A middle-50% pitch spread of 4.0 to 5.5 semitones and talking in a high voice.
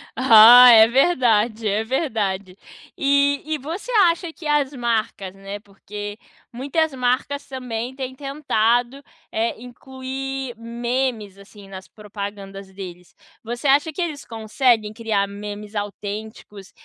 Yes: average, 4.5 semitones; high, 235 Hz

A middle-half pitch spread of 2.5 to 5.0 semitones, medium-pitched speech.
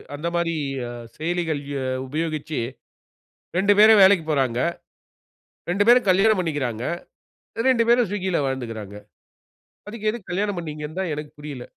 No: wide, 5.6 semitones; medium, 165 Hz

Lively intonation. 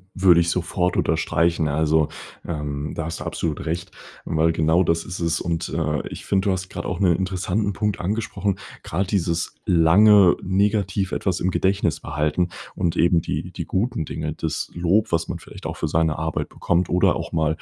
No: average, 2.8 semitones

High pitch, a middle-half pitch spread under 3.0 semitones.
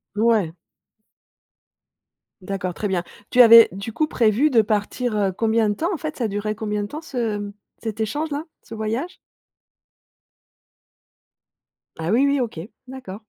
No: high, 220 Hz; average, 3.5 semitones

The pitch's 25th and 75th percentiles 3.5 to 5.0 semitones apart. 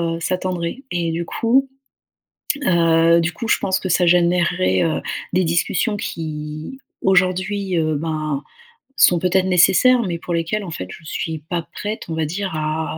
No: average, 2.7 semitones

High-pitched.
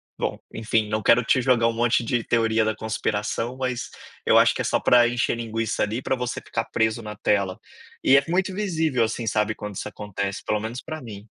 No: low, 115 Hz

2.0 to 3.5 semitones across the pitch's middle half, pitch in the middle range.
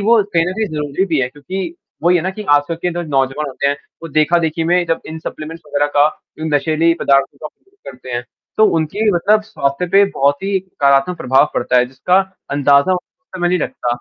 No: average, 4.3 semitones; medium, 160 Hz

